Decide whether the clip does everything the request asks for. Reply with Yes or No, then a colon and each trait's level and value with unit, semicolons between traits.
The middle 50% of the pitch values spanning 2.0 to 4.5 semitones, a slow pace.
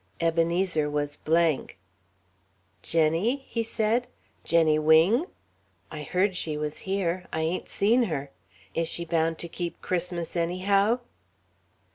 Yes: average, 3.6 semitones; slow, 120 wpm